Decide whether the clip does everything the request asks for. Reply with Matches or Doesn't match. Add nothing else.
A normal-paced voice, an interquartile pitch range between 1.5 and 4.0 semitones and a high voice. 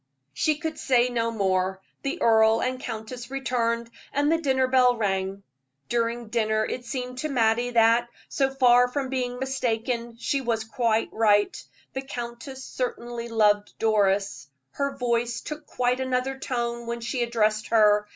Matches